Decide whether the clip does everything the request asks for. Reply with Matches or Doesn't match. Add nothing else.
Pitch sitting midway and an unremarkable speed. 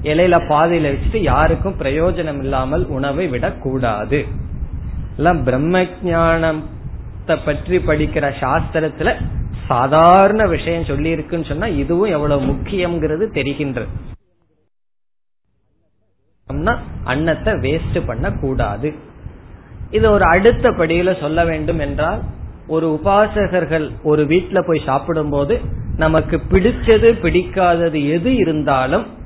Matches